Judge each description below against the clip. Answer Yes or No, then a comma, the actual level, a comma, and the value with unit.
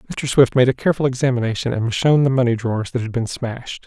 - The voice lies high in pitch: No, low, 125 Hz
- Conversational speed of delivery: No, fast, 250 wpm